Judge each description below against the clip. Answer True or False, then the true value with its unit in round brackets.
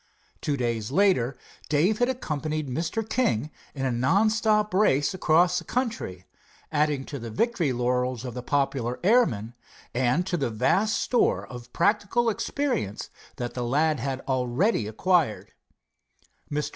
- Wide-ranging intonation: True (8.3 semitones)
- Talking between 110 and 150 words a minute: True (145 wpm)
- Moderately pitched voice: True (145 Hz)